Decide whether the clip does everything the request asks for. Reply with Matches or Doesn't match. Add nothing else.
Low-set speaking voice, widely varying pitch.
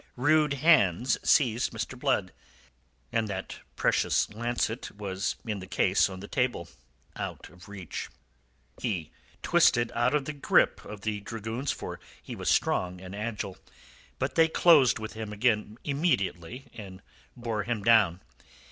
Doesn't match